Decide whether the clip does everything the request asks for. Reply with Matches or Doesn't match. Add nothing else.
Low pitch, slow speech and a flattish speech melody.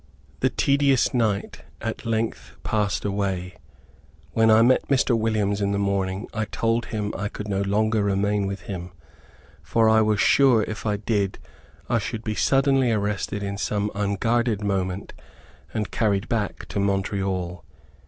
Doesn't match